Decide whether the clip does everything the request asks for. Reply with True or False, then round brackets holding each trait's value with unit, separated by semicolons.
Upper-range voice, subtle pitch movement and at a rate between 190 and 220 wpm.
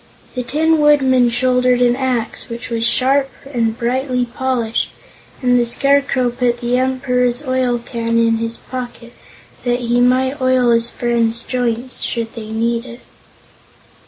False (245 Hz; 1.6 semitones; 145 wpm)